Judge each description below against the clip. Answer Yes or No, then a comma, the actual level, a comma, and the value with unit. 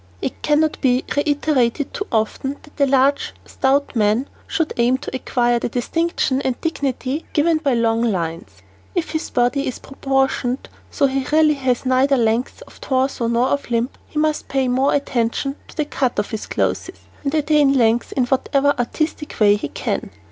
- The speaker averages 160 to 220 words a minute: Yes, average, 175 wpm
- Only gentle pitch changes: No, average, 3.0 semitones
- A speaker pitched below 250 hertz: No, very high, 265 Hz